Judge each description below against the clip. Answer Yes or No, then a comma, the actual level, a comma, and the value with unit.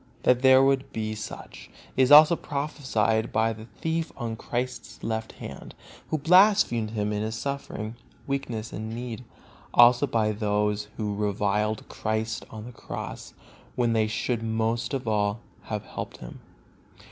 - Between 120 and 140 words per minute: No, average, 150 wpm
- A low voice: Yes, low, 115 Hz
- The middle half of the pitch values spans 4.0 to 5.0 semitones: No, average, 3.2 semitones